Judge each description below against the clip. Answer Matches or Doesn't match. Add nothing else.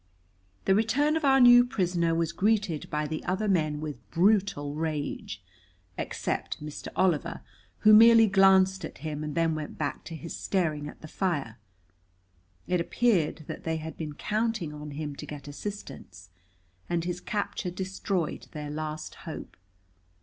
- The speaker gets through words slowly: Doesn't match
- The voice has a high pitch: Doesn't match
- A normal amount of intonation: Matches